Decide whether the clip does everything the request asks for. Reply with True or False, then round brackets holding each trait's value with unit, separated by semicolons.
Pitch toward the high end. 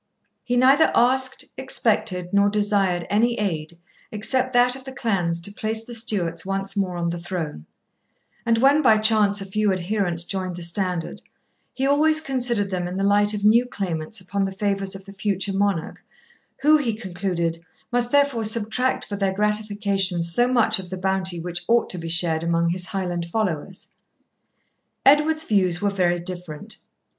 True (200 Hz)